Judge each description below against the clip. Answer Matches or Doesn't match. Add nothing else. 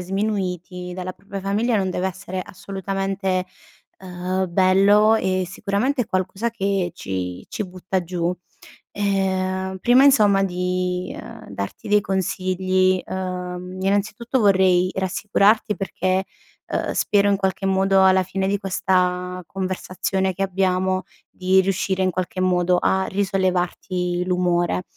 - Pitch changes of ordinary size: Doesn't match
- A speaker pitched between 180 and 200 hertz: Matches